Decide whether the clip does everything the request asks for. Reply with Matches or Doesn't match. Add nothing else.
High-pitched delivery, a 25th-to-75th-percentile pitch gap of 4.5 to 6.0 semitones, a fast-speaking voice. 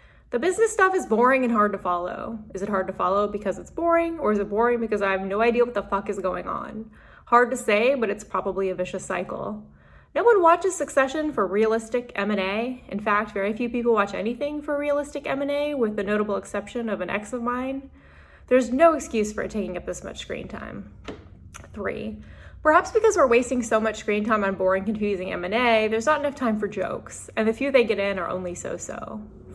Matches